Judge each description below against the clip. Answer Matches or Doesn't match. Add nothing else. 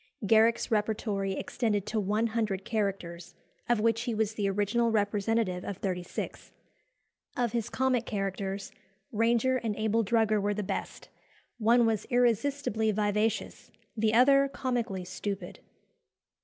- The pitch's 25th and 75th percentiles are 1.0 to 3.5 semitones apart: Matches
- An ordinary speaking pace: Doesn't match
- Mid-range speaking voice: Doesn't match